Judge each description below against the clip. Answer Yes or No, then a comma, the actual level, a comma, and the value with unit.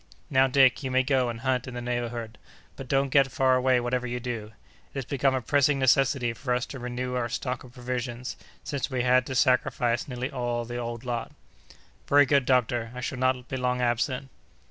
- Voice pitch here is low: Yes, low, 125 Hz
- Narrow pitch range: Yes, narrow, 1.5 semitones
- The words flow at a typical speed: No, fast, 210 wpm